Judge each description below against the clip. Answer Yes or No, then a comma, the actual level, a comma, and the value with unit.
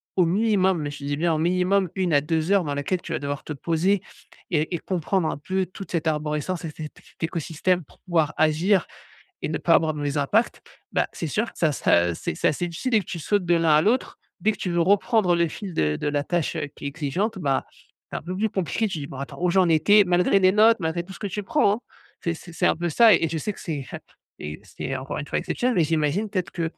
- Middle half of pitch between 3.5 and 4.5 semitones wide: Yes, average, 3.9 semitones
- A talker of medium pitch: Yes, medium, 170 Hz